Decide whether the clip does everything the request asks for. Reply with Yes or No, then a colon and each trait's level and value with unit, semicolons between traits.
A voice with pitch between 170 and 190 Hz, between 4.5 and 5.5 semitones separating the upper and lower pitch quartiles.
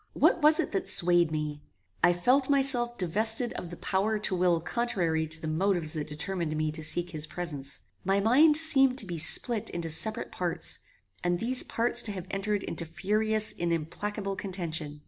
Yes: medium, 185 Hz; average, 5.2 semitones